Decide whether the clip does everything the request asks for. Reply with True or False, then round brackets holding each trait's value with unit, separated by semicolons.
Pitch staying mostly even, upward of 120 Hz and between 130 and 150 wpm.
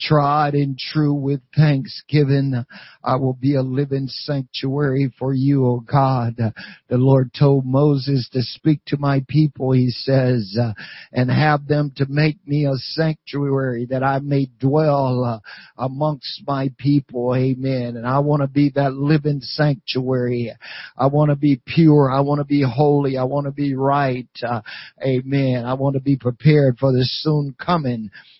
False (2.0 semitones; 135 Hz; 165 wpm)